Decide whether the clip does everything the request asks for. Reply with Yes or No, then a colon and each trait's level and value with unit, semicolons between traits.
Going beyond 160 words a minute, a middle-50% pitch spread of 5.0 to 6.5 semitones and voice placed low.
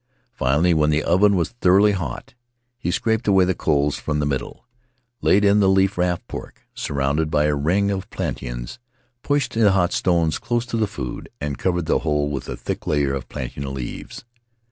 Yes: average, 190 wpm; average, 5.3 semitones; very low, 85 Hz